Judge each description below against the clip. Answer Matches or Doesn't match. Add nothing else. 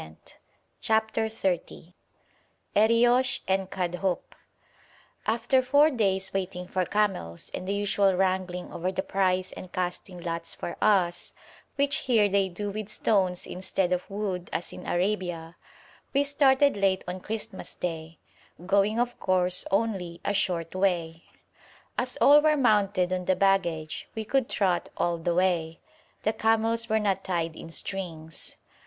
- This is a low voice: Doesn't match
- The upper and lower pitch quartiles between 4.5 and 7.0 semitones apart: Doesn't match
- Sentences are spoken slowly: Doesn't match